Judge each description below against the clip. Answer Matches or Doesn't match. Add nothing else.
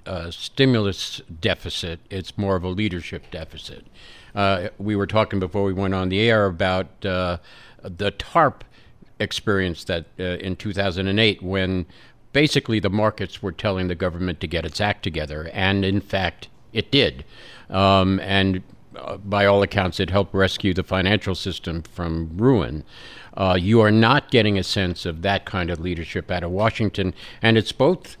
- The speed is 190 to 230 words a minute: Doesn't match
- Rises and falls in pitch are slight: Matches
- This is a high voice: Doesn't match